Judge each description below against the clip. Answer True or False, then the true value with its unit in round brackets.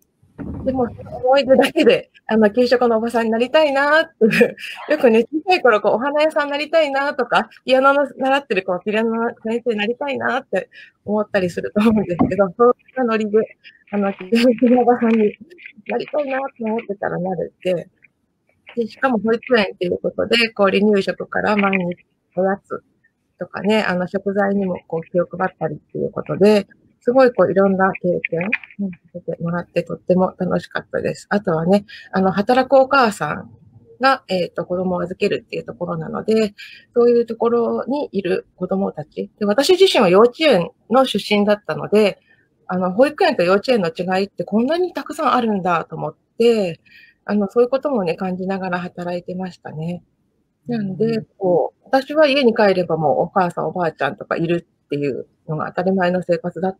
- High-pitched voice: True (210 Hz)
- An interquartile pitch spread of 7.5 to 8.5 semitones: False (5.5 semitones)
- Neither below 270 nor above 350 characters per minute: False (380 characters per minute)